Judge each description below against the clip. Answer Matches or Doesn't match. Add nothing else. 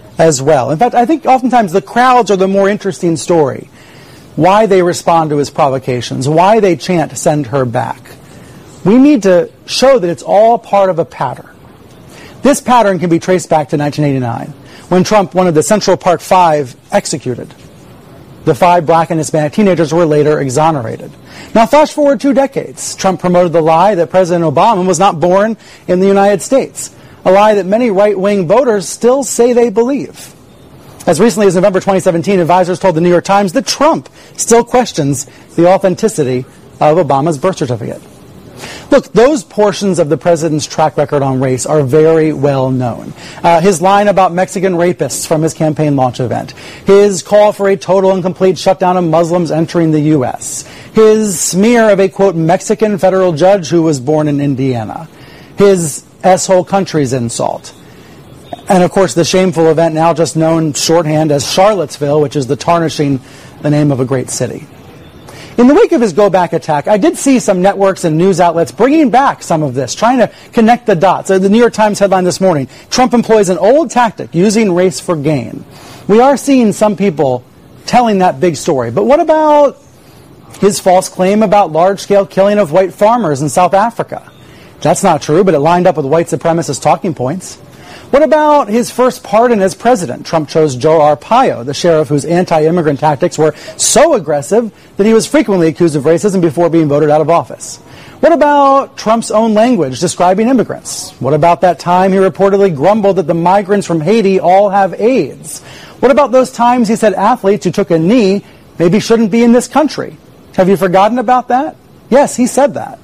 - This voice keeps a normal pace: Matches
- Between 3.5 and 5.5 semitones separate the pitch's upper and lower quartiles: Matches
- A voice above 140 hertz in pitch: Matches